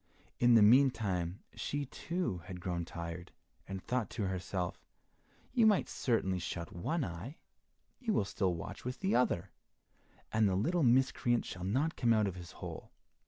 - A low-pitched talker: Yes, low, 105 Hz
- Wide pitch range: Yes, wide, 6.5 semitones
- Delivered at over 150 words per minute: Yes, average, 165 wpm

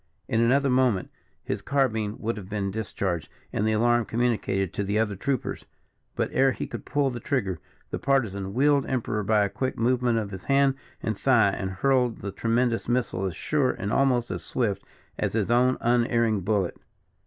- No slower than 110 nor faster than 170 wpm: No, average, 185 wpm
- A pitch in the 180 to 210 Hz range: No, low, 115 Hz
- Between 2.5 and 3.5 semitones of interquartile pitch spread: No, average, 4.0 semitones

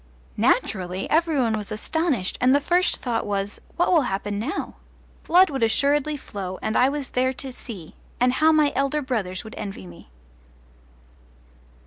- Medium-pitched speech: No, very high, 250 Hz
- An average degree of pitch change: No, wide, 6.3 semitones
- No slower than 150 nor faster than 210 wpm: Yes, average, 160 wpm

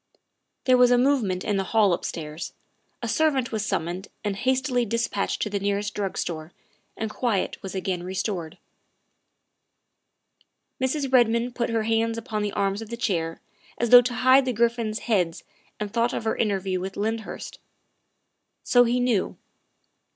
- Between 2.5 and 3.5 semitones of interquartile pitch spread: No, average, 3.9 semitones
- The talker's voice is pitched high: Yes, high, 220 Hz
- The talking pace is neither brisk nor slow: Yes, average, 165 wpm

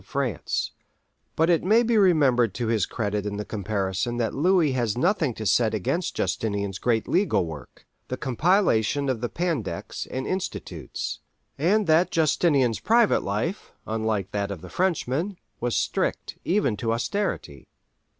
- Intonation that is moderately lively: No, wide, 8.5 semitones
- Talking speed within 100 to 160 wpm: Yes, average, 150 wpm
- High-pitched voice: No, low, 125 Hz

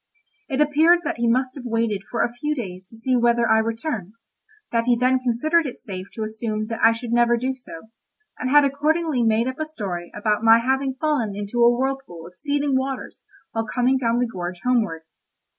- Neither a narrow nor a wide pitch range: Yes, average, 3.2 semitones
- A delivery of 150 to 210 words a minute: Yes, fast, 205 wpm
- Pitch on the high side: Yes, high, 240 Hz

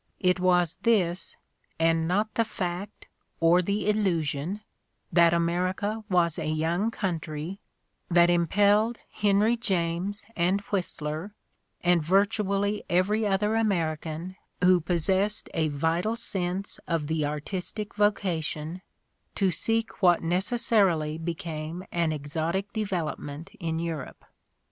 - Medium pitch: Yes, medium, 180 Hz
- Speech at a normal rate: No, slow, 110 wpm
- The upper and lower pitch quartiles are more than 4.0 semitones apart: No, average, 3.7 semitones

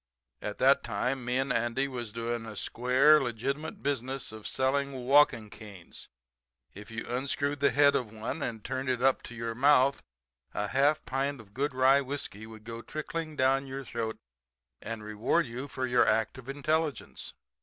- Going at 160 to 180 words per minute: Yes, average, 175 wpm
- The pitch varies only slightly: No, average, 3.3 semitones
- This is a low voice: Yes, low, 130 Hz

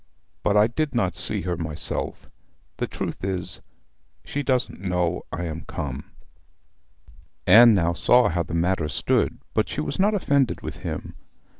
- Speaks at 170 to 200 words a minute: No, average, 155 wpm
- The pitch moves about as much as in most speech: No, wide, 6.2 semitones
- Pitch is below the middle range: Yes, very low, 90 Hz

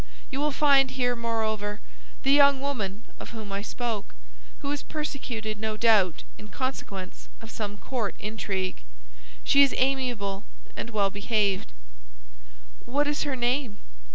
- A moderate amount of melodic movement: Yes, average, 4.6 semitones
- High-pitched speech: Yes, high, 230 Hz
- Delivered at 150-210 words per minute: No, average, 140 wpm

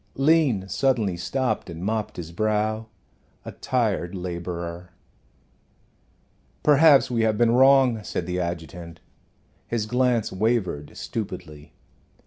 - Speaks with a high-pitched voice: No, low, 105 Hz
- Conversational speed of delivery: No, slow, 110 wpm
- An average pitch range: No, wide, 5.7 semitones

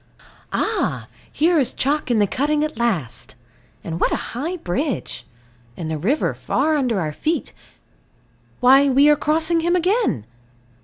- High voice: Yes, very high, 275 Hz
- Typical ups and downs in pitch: No, wide, 7.4 semitones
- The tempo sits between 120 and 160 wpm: Yes, average, 150 wpm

